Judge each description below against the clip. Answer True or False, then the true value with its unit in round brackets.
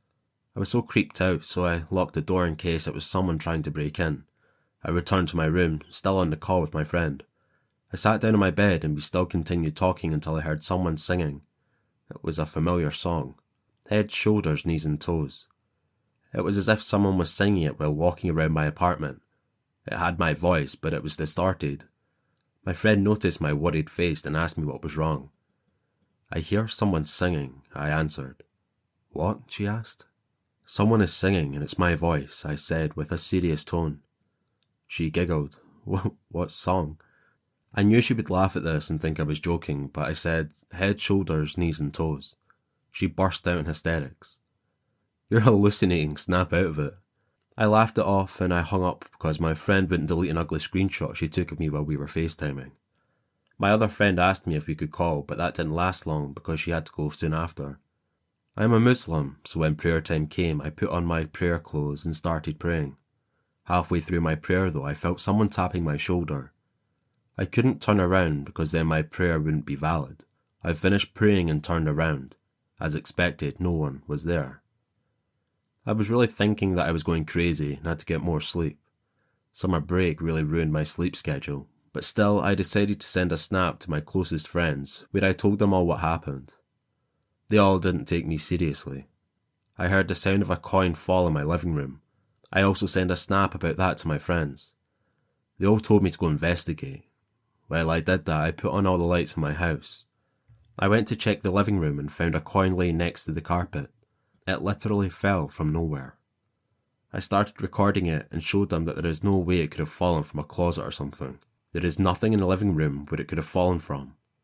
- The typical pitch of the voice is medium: False (85 Hz)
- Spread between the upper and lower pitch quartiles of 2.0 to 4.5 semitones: True (3.7 semitones)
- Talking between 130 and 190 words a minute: False (205 wpm)